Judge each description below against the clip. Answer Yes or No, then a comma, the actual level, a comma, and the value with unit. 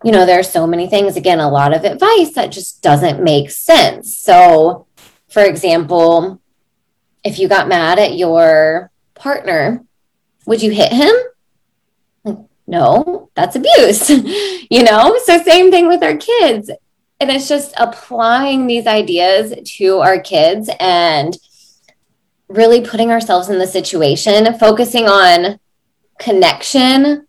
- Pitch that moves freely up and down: Yes, wide, 7.6 semitones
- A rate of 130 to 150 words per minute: Yes, slow, 135 wpm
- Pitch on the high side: Yes, high, 220 Hz